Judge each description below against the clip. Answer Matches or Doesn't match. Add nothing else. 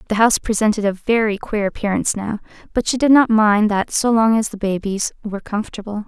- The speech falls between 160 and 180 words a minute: Doesn't match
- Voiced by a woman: Matches